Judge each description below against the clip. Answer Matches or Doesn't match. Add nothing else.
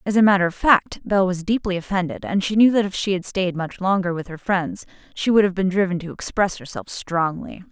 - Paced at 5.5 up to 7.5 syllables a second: Matches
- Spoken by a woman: Matches